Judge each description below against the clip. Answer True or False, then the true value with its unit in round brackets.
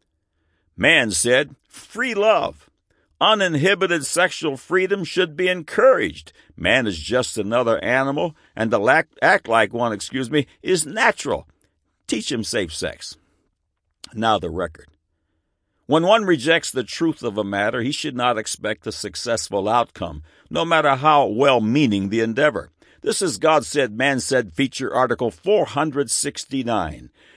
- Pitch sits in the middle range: False (130 Hz)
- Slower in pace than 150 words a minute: True (135 wpm)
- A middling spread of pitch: False (8.0 semitones)